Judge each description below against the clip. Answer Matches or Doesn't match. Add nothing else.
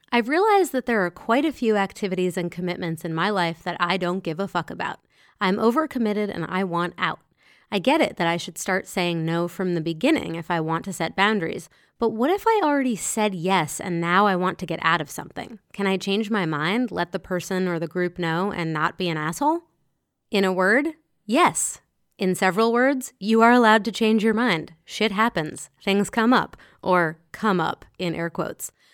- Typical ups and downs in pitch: Matches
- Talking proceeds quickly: Matches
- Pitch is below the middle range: Doesn't match